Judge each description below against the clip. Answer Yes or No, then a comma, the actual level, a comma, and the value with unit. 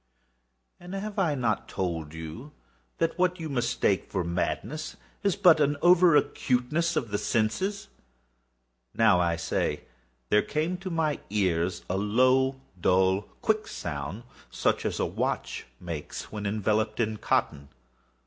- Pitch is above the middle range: No, low, 110 Hz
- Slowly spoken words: Yes, slow, 130 wpm